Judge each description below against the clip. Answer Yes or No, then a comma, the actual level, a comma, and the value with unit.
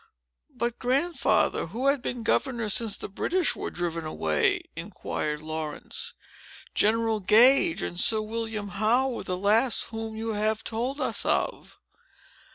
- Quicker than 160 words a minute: No, average, 140 wpm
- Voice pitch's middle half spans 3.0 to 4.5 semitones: Yes, average, 3.7 semitones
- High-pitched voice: Yes, high, 220 Hz